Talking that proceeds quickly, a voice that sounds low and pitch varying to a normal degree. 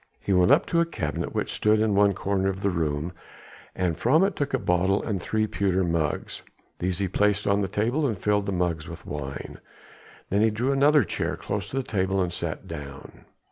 Yes: fast, 215 wpm; low, 100 Hz; average, 3.4 semitones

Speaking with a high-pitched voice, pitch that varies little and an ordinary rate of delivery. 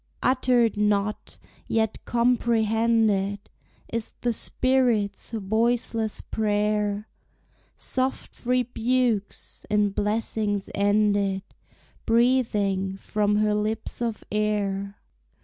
No: high, 215 Hz; narrow, 2.3 semitones; slow, 80 wpm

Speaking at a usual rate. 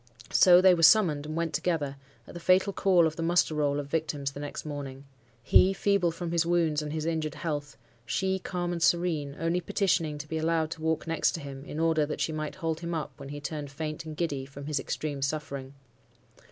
No: fast, 220 wpm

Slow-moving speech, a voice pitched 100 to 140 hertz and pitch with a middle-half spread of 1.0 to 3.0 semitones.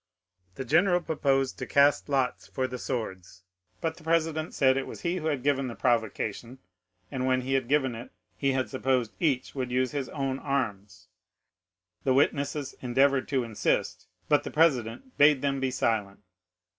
No: average, 170 wpm; low, 135 Hz; narrow, 2.5 semitones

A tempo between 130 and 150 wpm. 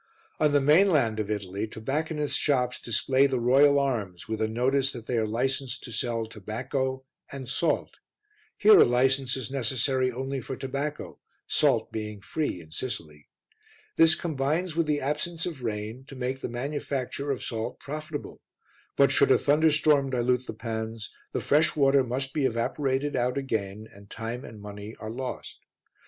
No: average, 165 wpm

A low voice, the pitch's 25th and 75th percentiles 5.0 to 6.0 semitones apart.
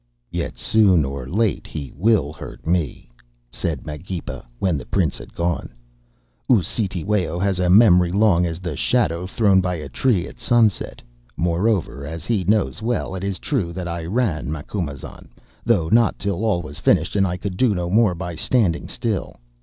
No: very low, 90 Hz; average, 3.9 semitones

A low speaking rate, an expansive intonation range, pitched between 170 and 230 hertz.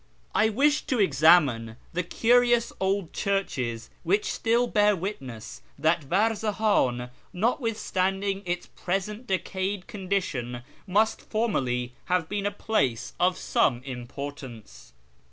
Yes: slow, 110 wpm; wide, 7.7 semitones; medium, 185 Hz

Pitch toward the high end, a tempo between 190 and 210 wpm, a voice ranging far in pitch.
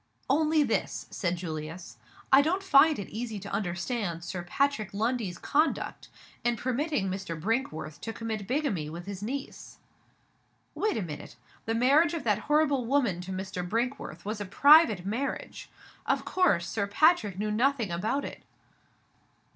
No: high, 220 Hz; average, 150 wpm; wide, 7.1 semitones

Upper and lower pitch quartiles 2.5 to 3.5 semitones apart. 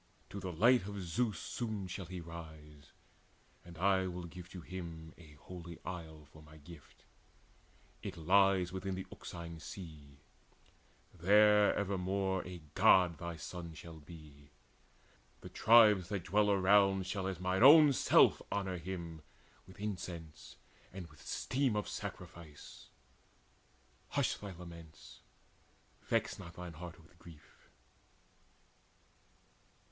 Yes: average, 3.0 semitones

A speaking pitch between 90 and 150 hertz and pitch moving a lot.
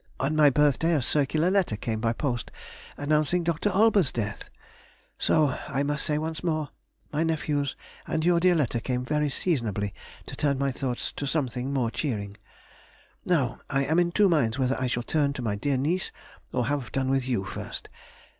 No: medium, 140 Hz; average, 4.1 semitones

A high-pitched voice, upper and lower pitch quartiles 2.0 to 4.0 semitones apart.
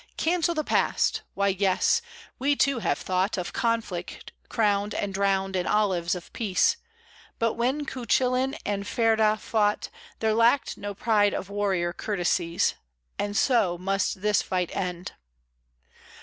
Yes: high, 205 Hz; average, 3.4 semitones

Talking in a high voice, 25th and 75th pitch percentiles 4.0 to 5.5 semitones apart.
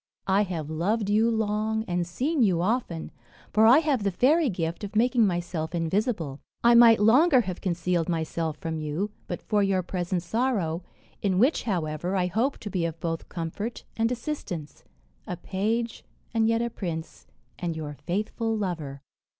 Yes: high, 195 Hz; average, 5.2 semitones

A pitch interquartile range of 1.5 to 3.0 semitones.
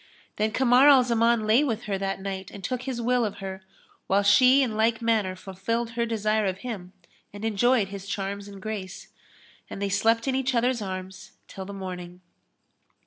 No: average, 3.4 semitones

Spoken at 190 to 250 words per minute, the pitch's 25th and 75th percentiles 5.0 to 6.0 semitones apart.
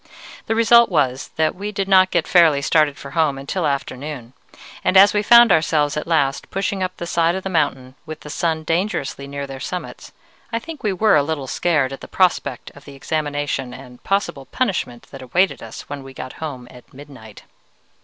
Yes: average, 200 wpm; wide, 5.4 semitones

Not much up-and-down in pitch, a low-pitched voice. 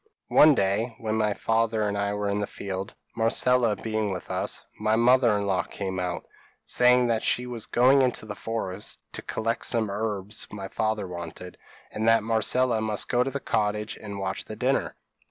Yes: narrow, 2.3 semitones; low, 110 Hz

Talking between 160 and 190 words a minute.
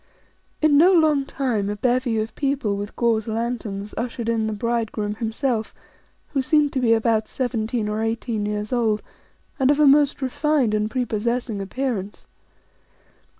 No: average, 150 wpm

